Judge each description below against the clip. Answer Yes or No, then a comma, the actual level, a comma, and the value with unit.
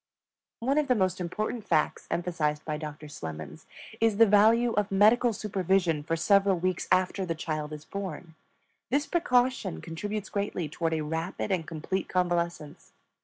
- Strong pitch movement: No, average, 4.5 semitones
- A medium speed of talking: Yes, average, 155 wpm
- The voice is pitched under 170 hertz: No, medium, 185 Hz